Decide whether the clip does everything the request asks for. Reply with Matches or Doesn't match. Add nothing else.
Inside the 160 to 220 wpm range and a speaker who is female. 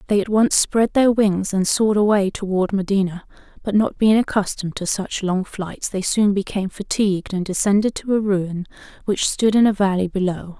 Matches